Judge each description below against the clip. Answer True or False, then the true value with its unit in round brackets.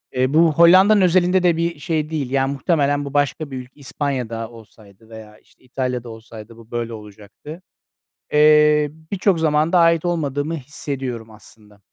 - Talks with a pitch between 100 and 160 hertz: True (140 Hz)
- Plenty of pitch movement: True (5.7 semitones)